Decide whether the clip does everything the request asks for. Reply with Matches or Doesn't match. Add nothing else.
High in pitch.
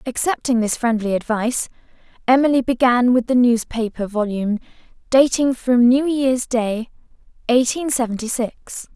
Matches